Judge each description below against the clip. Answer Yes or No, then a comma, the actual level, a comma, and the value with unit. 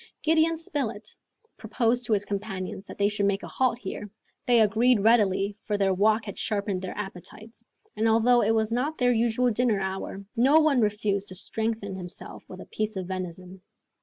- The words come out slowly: No, average, 185 wpm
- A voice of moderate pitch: No, high, 215 Hz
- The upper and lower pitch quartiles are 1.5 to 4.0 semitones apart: Yes, average, 3.1 semitones